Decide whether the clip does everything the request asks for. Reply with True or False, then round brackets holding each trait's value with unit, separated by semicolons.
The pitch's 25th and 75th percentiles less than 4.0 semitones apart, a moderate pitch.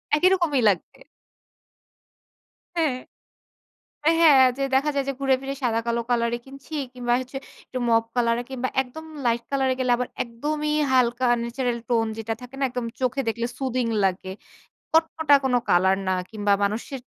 False (2.8 semitones; 250 Hz)